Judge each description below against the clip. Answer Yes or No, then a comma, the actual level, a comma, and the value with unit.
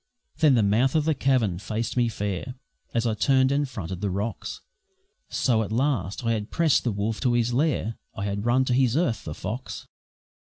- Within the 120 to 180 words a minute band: No, average, 200 wpm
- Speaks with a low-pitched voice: Yes, low, 115 Hz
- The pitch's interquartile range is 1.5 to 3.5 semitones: No, average, 4.1 semitones